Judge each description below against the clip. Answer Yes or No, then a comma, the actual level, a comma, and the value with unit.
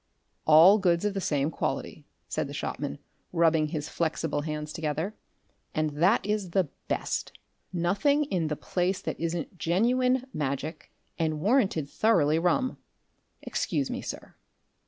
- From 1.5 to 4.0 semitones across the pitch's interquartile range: No, average, 4.4 semitones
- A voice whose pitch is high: No, medium, 170 Hz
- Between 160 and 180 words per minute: No, slow, 135 wpm